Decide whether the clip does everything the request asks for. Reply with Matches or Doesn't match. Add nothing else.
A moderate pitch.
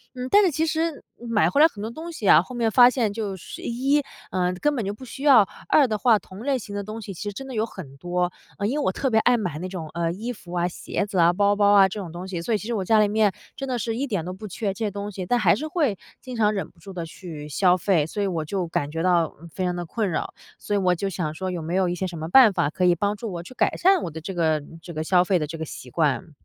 Doesn't match